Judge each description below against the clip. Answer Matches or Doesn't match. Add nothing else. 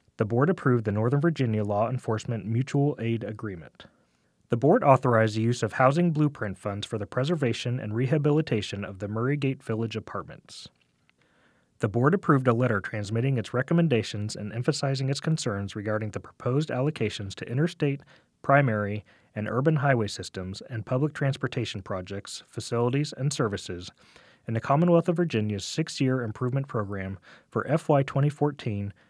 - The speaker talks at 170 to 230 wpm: Doesn't match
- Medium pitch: Doesn't match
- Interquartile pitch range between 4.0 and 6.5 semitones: Matches